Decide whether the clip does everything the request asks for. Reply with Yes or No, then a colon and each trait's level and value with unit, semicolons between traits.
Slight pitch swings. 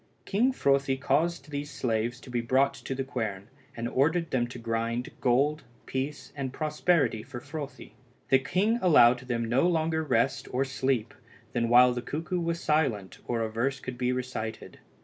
No: average, 3.9 semitones